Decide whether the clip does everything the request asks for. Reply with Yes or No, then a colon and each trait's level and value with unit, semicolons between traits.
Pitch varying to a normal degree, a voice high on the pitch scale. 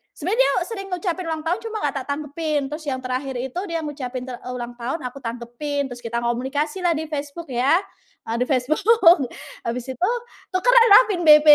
Yes: average, 5.0 semitones; very high, 290 Hz